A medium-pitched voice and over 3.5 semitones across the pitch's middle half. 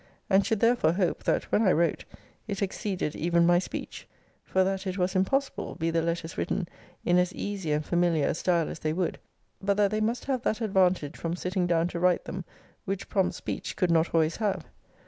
No: medium, 180 Hz; average, 2.8 semitones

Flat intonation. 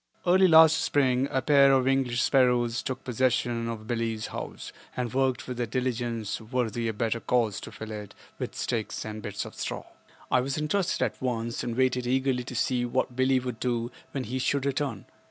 Yes: narrow, 2.3 semitones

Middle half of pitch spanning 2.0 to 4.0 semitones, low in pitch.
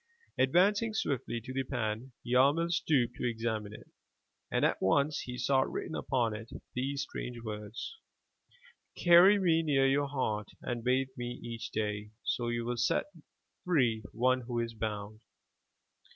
Yes: average, 3.7 semitones; low, 125 Hz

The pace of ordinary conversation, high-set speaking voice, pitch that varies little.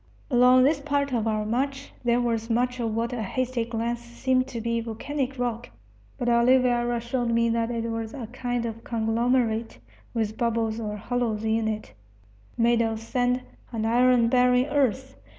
Yes: average, 170 wpm; high, 235 Hz; narrow, 1.7 semitones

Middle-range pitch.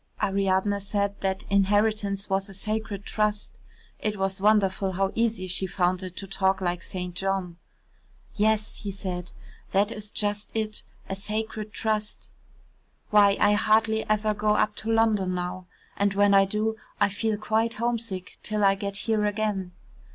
No: high, 205 Hz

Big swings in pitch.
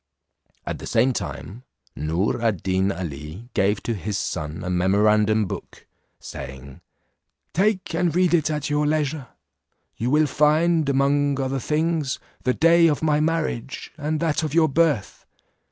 Yes: wide, 7.4 semitones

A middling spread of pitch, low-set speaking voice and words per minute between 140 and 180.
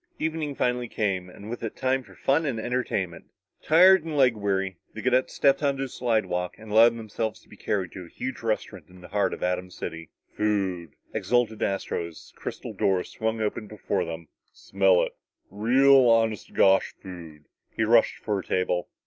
No: average, 4.9 semitones; low, 110 Hz; average, 190 wpm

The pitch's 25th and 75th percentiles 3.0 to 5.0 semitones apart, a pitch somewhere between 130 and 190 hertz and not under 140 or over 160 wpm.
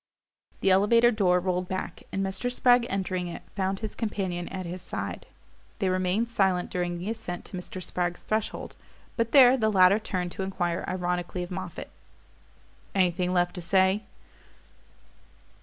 No: narrow, 2.5 semitones; medium, 185 Hz; average, 155 wpm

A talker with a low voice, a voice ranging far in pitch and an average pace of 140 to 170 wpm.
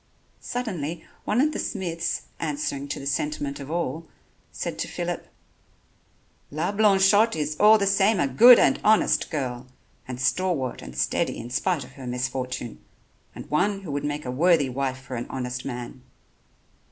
No: medium, 145 Hz; wide, 6.7 semitones; average, 165 wpm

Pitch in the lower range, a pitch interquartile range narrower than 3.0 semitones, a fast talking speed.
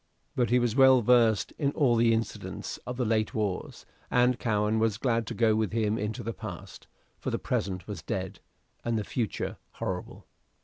No: low, 110 Hz; narrow, 2.4 semitones; average, 185 wpm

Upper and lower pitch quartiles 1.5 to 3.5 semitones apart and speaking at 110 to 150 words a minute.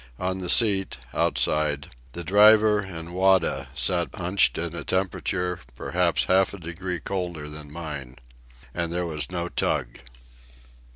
Yes: average, 2.8 semitones; slow, 135 wpm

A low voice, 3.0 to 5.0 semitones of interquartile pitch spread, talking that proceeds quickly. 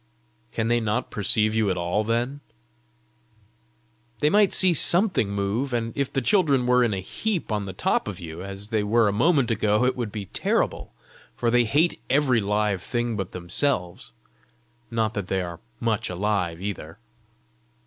No: low, 110 Hz; average, 4.0 semitones; average, 170 wpm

